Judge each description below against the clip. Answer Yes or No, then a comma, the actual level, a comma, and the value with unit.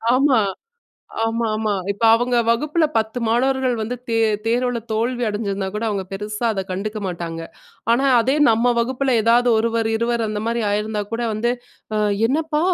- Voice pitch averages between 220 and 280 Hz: Yes, high, 230 Hz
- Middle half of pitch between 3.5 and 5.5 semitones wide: No, narrow, 2.4 semitones